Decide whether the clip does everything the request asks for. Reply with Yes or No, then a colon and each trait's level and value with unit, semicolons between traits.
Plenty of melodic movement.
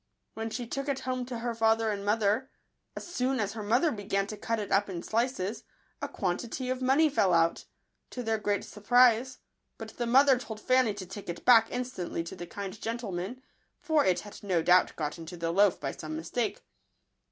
No: average, 4.6 semitones